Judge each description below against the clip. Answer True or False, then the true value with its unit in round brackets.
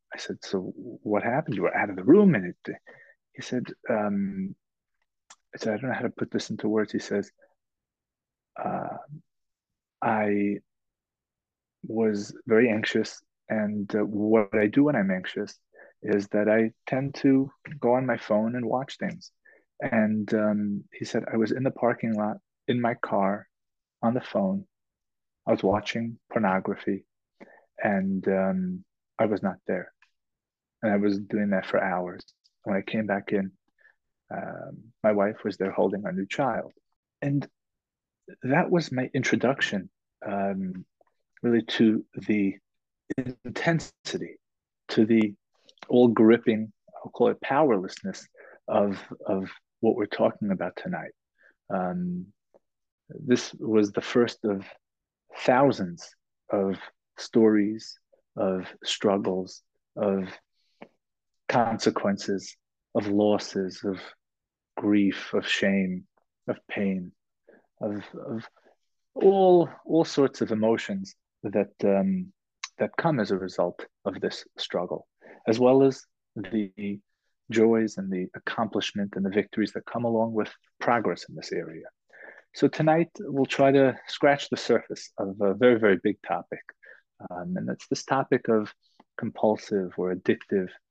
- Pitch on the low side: True (105 Hz)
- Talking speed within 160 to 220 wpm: False (135 wpm)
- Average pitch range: True (3.9 semitones)